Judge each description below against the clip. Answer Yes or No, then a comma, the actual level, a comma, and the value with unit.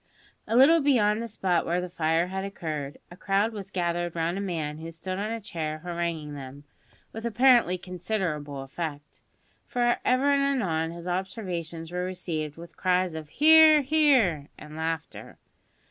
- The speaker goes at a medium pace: Yes, average, 160 wpm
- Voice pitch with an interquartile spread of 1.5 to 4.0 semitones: No, average, 5.1 semitones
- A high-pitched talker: No, medium, 180 Hz